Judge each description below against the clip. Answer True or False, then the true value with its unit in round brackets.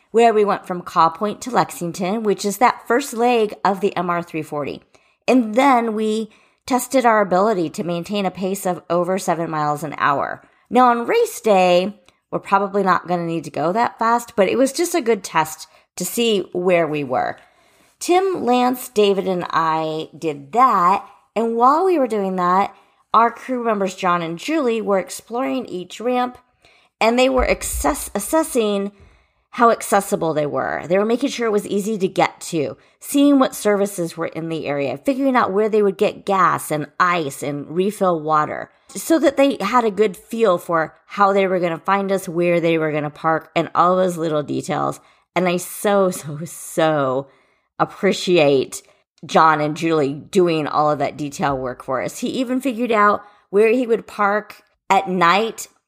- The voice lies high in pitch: True (195 Hz)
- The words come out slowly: False (180 wpm)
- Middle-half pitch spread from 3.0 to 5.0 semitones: False (5.5 semitones)